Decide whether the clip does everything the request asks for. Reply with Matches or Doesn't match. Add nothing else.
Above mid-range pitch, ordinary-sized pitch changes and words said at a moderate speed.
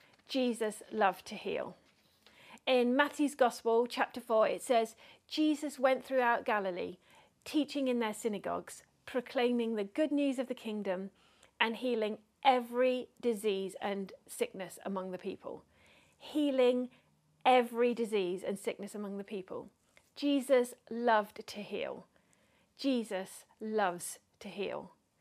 Doesn't match